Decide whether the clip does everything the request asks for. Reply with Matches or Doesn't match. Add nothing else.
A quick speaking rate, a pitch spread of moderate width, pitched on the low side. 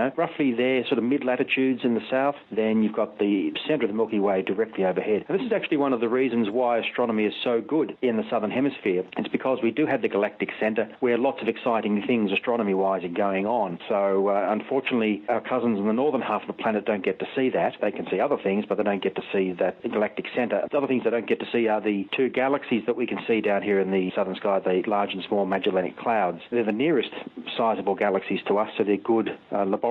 Matches